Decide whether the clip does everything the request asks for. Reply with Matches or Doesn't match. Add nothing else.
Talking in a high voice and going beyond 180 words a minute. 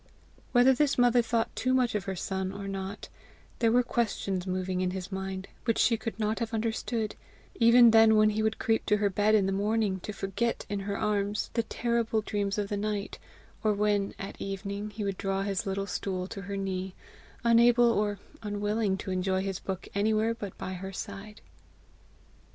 Matches